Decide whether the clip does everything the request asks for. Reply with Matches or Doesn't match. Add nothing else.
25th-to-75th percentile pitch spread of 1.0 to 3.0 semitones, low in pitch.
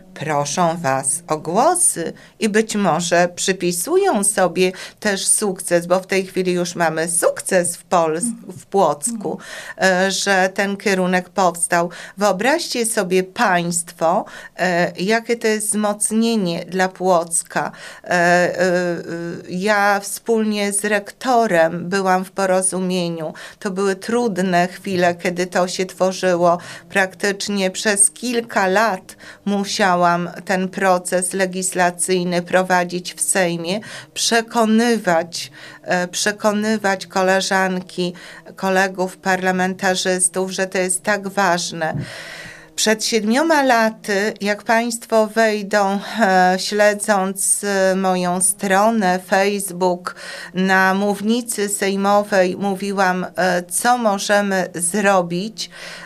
Doesn't match